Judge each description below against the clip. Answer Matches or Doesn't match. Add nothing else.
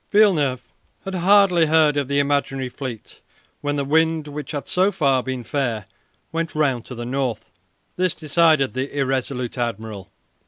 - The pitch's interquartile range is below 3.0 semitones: Doesn't match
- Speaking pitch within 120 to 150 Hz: Matches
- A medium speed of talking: Matches